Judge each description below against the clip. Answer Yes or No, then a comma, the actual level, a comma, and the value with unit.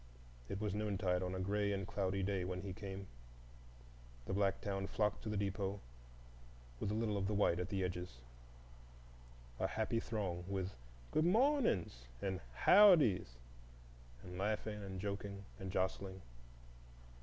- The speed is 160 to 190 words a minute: No, average, 145 wpm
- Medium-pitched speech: No, very low, 95 Hz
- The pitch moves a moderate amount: No, narrow, 2.3 semitones